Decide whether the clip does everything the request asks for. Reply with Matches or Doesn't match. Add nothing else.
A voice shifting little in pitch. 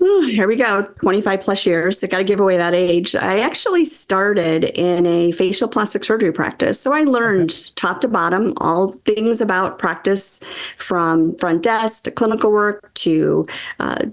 Doesn't match